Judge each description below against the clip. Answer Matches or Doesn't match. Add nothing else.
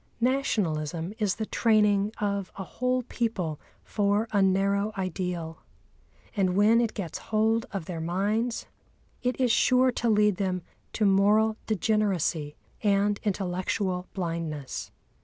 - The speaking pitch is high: Matches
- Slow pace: Matches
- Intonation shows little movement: Doesn't match